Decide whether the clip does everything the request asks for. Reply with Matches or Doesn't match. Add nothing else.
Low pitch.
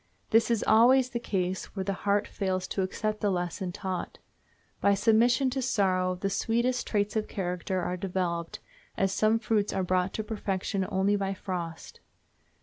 Doesn't match